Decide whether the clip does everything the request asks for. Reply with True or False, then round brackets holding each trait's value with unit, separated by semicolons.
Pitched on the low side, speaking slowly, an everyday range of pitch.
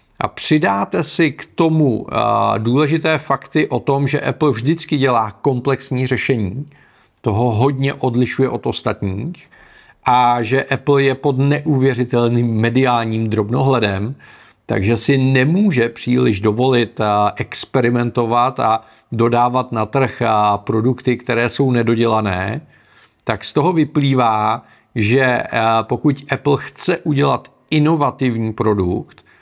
True (125 Hz; 110 wpm; 3.5 semitones)